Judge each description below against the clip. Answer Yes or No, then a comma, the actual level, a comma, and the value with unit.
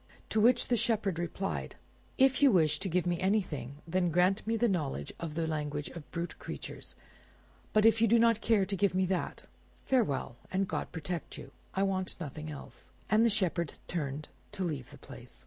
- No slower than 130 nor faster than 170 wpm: No, average, 190 wpm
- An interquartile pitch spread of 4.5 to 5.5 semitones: Yes, average, 5.2 semitones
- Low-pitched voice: No, medium, 185 Hz